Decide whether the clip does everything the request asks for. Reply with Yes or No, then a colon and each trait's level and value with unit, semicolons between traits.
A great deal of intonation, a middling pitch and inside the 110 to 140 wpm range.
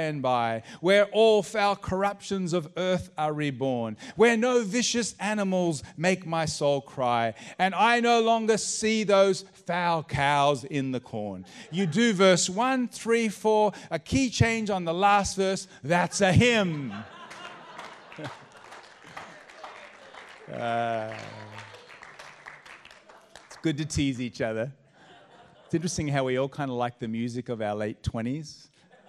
Yes: wide, 7.4 semitones; medium, 170 Hz; slow, 135 wpm